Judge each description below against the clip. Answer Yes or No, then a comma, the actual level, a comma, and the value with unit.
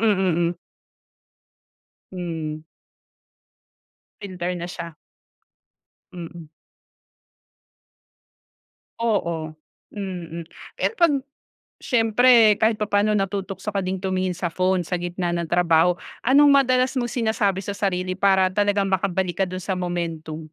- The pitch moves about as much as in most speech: Yes, average, 3.0 semitones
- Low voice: No, medium, 185 Hz